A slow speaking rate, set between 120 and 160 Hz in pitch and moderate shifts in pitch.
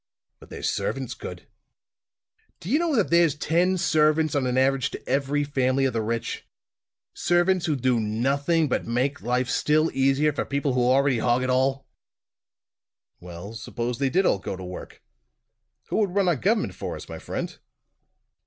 No: average, 170 wpm; low, 135 Hz; average, 4.3 semitones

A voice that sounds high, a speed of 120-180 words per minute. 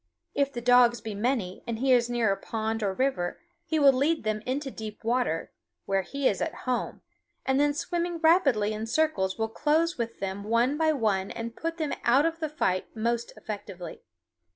No: high, 240 Hz; average, 195 wpm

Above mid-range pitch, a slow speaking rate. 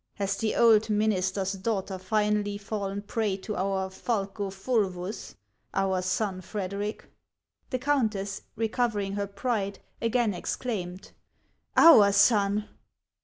Yes: high, 205 Hz; slow, 120 wpm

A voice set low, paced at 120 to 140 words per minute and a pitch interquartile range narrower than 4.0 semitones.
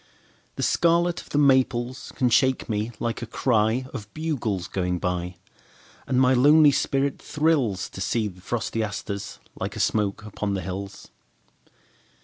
No: low, 115 Hz; slow, 135 wpm; average, 5.0 semitones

